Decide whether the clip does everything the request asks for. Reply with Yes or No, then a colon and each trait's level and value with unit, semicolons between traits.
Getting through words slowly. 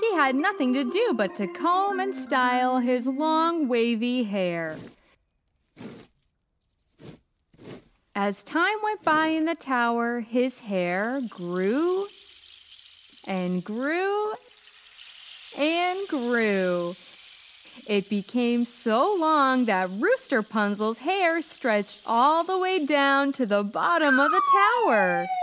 Yes: slow, 110 wpm